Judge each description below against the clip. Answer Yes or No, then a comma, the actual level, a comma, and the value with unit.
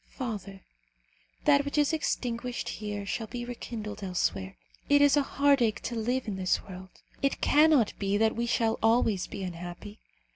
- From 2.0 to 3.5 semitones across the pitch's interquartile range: No, average, 4.7 semitones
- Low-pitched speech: No, high, 225 Hz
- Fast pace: No, average, 160 wpm